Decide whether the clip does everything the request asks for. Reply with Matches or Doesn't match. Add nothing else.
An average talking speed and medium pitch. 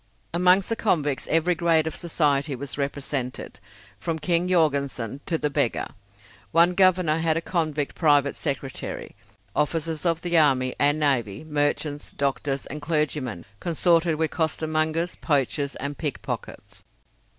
Doesn't match